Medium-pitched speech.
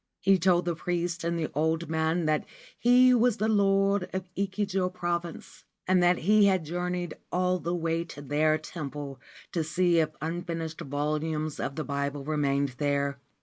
Yes: medium, 170 Hz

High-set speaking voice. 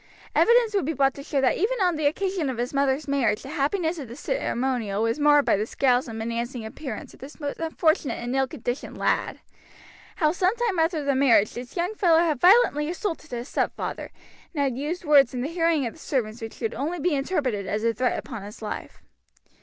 Yes: very high, 280 Hz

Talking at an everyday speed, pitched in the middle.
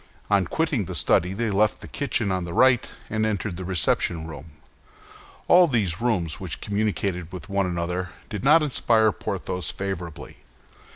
No: average, 160 wpm; low, 100 Hz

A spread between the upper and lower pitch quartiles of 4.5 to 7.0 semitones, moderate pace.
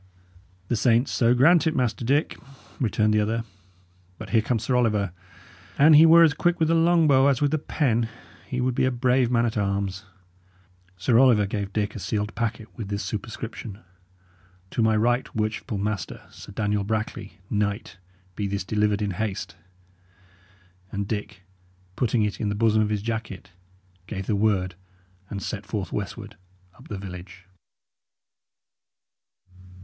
No: average, 3.4 semitones; average, 160 wpm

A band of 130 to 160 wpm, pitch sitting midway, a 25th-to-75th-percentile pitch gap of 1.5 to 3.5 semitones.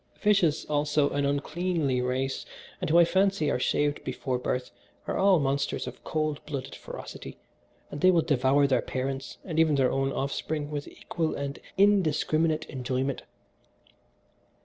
Yes: average, 150 wpm; medium, 145 Hz; average, 2.9 semitones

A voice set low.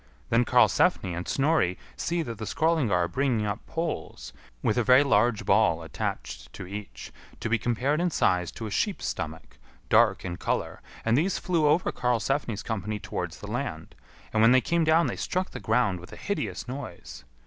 Yes: low, 120 Hz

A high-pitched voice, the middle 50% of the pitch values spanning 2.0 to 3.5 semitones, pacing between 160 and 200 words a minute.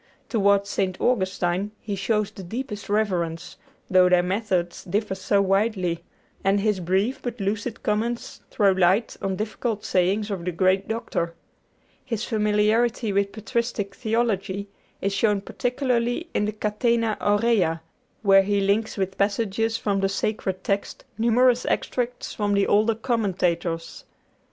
No: high, 205 Hz; average, 2.8 semitones; slow, 135 wpm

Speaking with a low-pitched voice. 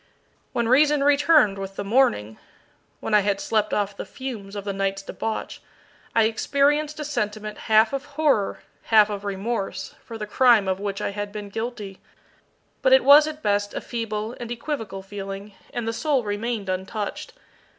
No: high, 215 Hz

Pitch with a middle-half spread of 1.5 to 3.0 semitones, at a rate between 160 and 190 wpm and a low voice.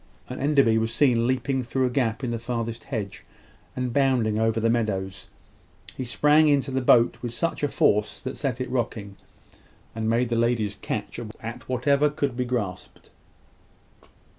Yes: average, 2.7 semitones; average, 165 wpm; low, 120 Hz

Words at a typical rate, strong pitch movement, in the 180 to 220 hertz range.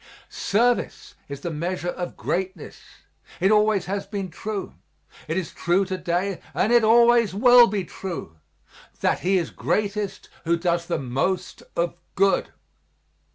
No: average, 145 wpm; average, 3.4 semitones; high, 190 Hz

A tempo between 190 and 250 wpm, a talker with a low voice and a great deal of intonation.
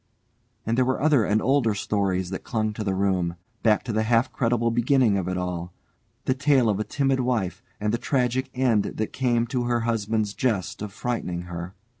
No: average, 200 wpm; low, 110 Hz; average, 4.0 semitones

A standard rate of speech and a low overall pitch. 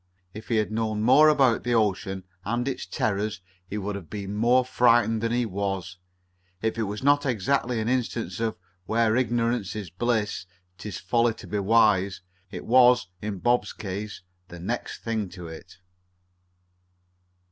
Yes: average, 160 wpm; low, 110 Hz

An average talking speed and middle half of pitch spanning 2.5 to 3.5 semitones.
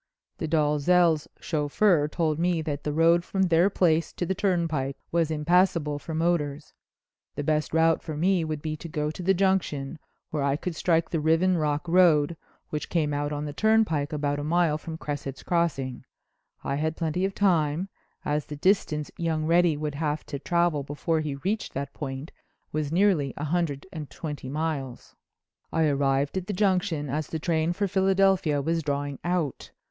Yes: average, 180 wpm; average, 2.9 semitones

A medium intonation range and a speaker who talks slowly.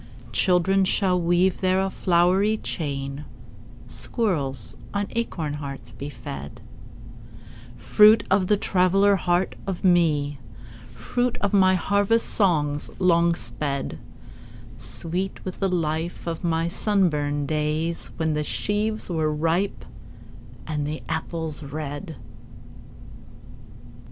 Yes: average, 4.2 semitones; slow, 110 wpm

